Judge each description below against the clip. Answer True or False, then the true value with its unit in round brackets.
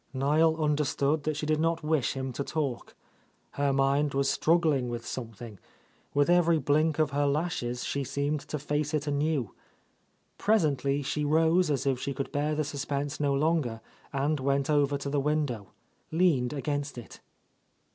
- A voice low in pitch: False (145 Hz)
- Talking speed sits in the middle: True (165 wpm)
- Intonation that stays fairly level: True (2.0 semitones)